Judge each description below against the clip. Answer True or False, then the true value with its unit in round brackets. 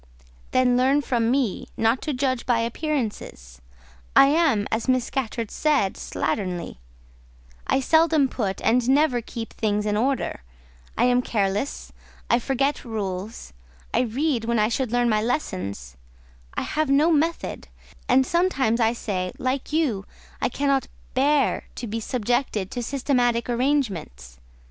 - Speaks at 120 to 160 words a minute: True (140 wpm)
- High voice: True (245 Hz)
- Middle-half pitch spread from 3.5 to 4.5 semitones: True (4.2 semitones)